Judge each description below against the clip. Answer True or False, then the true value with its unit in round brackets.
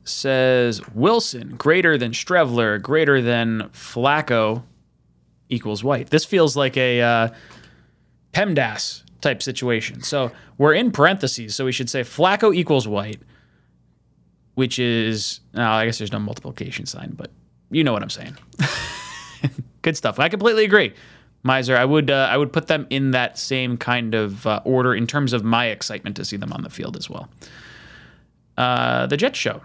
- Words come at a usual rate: True (165 wpm)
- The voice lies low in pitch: True (125 Hz)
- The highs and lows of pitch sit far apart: False (3.7 semitones)